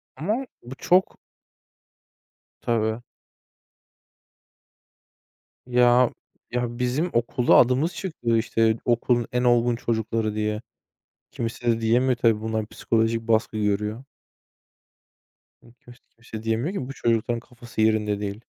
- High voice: No, low, 115 Hz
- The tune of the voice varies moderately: No, narrow, 1.8 semitones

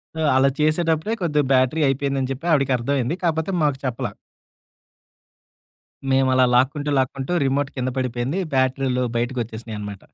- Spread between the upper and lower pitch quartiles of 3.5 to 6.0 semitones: No, narrow, 2.6 semitones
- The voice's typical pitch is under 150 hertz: Yes, low, 135 Hz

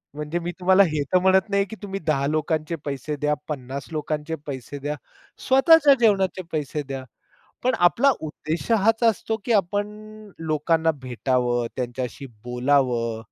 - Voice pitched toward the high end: No, medium, 155 Hz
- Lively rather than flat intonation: Yes, wide, 5.9 semitones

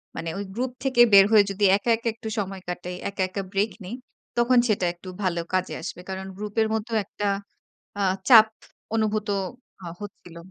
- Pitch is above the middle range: Yes, high, 205 Hz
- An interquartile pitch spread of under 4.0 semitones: Yes, average, 2.7 semitones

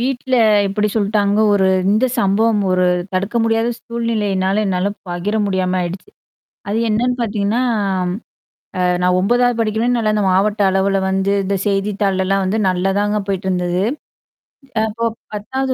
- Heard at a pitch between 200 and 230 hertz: Yes, high, 205 Hz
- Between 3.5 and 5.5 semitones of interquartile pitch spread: No, average, 2.7 semitones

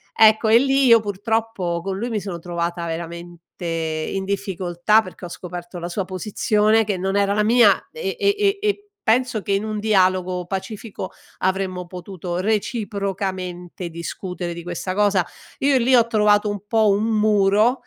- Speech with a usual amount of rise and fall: Yes, average, 3.5 semitones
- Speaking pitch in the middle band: No, high, 200 Hz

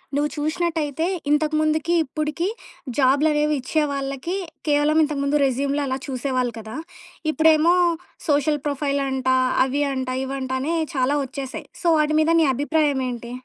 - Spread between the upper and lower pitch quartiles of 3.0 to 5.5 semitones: No, narrow, 2.6 semitones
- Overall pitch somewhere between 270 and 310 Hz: Yes, very high, 290 Hz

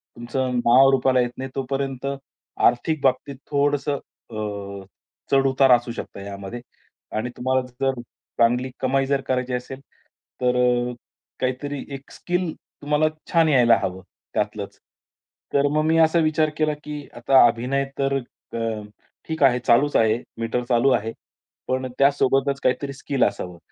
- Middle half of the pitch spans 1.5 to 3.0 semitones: Yes, narrow, 2.6 semitones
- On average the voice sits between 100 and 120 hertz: No, low, 130 Hz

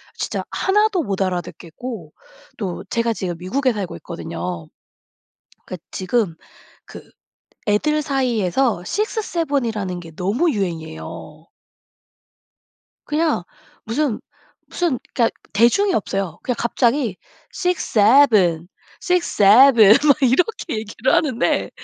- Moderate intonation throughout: No, wide, 7.3 semitones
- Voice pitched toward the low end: No, high, 225 Hz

